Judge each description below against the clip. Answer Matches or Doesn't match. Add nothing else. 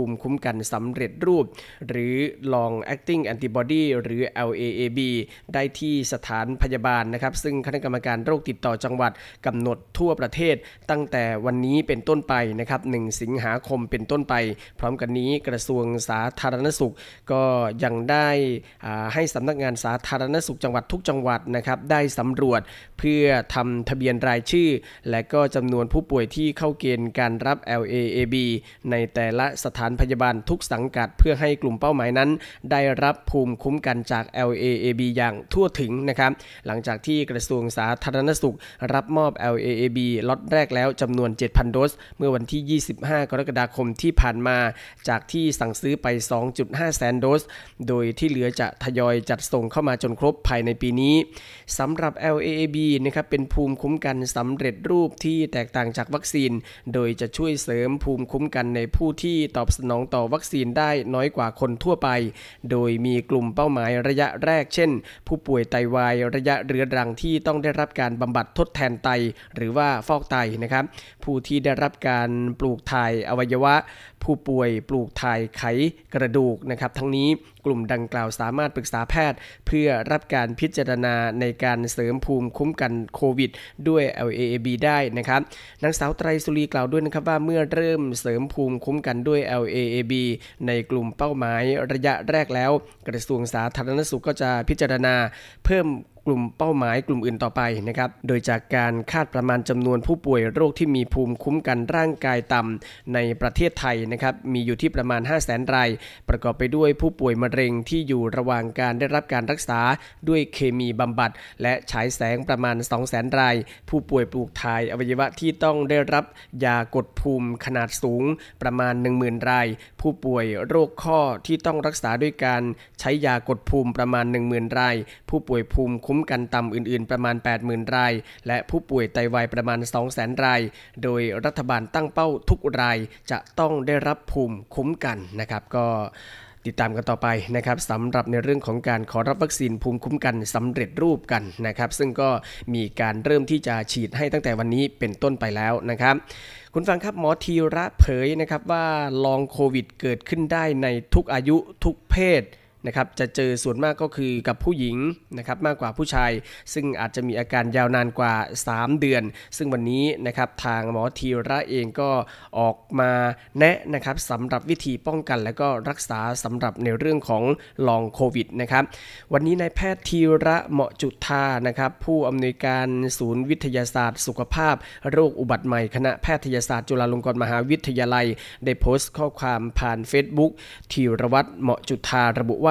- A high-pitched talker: Doesn't match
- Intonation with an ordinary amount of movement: Matches